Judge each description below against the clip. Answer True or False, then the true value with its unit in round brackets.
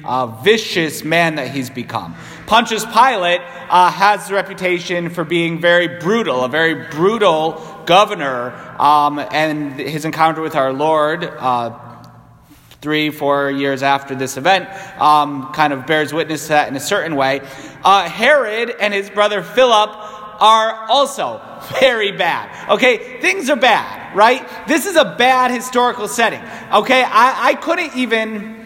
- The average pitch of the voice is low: False (175 Hz)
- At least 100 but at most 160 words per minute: True (150 wpm)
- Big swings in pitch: True (6.4 semitones)